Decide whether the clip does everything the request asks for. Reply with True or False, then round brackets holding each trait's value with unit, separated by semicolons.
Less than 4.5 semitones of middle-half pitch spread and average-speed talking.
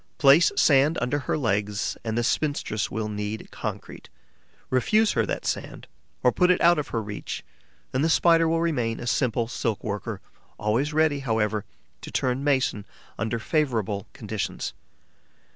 False (5.5 semitones; 155 wpm)